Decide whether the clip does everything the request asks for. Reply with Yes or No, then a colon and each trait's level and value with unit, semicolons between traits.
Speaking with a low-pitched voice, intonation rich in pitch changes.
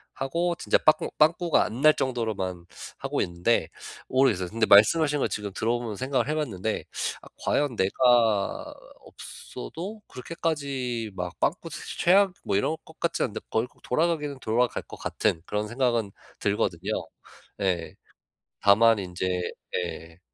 Yes: low, 115 Hz; wide, 6.7 semitones